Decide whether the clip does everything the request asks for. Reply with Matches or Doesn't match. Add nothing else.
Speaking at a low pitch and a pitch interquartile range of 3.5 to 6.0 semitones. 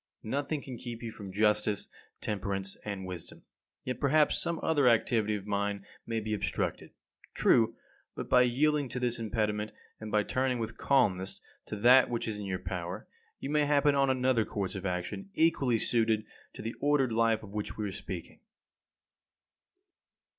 Matches